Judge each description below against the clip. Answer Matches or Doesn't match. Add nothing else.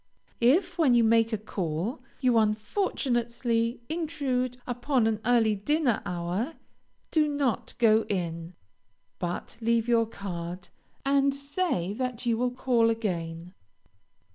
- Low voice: Doesn't match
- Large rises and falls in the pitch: Doesn't match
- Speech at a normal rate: Doesn't match